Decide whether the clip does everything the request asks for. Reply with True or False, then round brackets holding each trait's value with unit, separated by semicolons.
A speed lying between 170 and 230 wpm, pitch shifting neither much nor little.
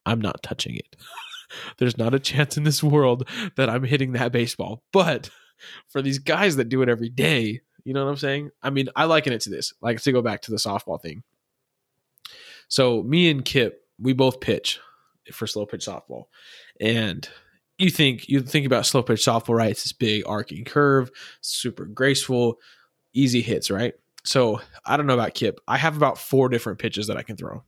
True (200 wpm; 3.4 semitones)